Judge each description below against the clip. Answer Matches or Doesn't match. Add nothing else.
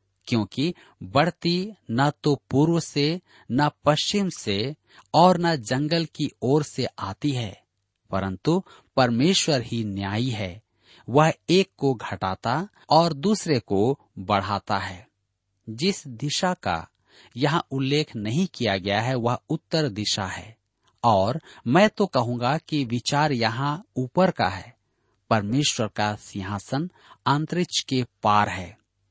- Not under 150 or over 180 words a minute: Doesn't match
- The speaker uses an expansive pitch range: Matches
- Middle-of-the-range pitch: Doesn't match